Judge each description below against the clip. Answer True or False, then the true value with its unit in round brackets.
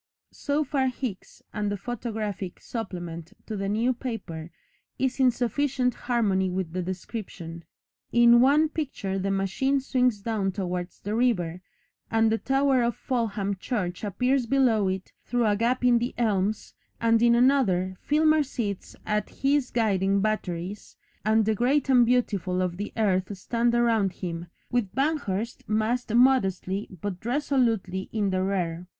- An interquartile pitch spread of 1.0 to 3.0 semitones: False (4.6 semitones)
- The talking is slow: False (150 wpm)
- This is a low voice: False (220 Hz)